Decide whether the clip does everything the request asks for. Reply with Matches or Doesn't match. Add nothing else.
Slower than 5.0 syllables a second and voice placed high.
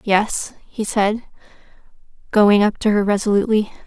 Matches